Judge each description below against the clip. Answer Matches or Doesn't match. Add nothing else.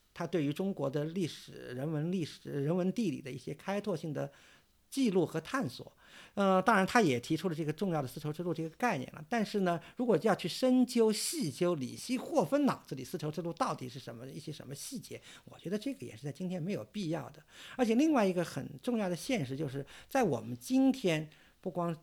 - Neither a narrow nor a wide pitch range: Doesn't match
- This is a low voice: Doesn't match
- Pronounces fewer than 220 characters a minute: Doesn't match